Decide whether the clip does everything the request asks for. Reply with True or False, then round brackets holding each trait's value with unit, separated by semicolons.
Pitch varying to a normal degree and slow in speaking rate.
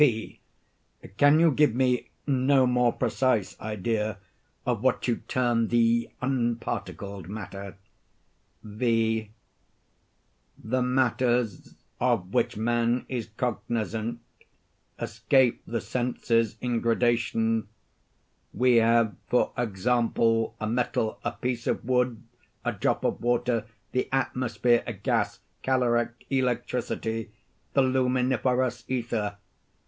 False (2.0 semitones; 105 wpm)